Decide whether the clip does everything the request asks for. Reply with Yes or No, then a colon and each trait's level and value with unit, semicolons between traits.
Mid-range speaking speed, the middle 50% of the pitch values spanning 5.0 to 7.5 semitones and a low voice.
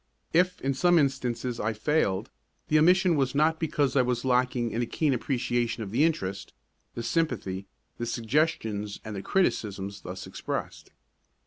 Yes: average, 155 wpm; wide, 5.5 semitones; low, 125 Hz